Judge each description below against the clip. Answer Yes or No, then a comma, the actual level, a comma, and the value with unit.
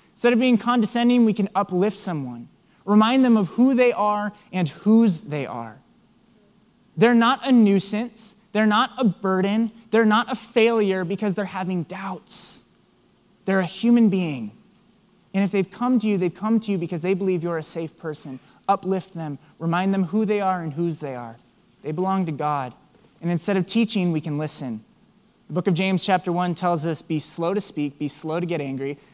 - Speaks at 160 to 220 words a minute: Yes, average, 195 wpm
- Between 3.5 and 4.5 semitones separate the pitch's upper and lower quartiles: Yes, average, 4.2 semitones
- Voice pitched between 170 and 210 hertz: Yes, high, 190 Hz